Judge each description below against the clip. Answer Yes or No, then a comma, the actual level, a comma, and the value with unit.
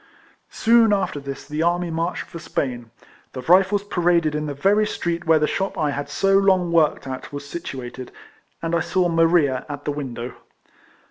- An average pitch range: Yes, average, 3.9 semitones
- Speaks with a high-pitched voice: No, medium, 165 Hz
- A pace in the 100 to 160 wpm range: No, average, 185 wpm